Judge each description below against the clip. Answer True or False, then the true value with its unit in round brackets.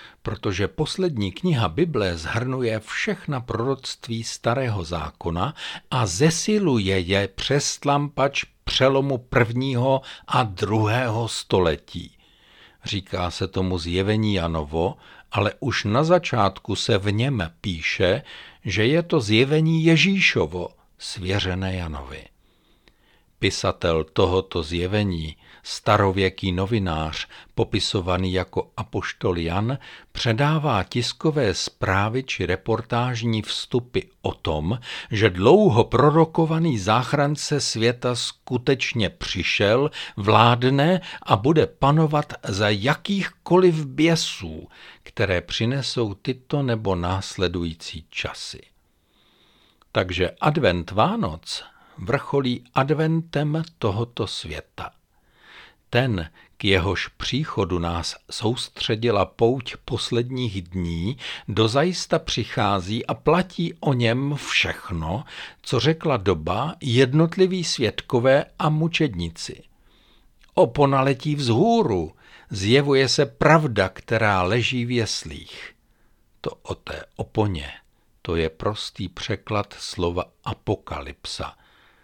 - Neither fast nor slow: False (90 wpm)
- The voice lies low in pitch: True (120 Hz)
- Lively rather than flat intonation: True (6.7 semitones)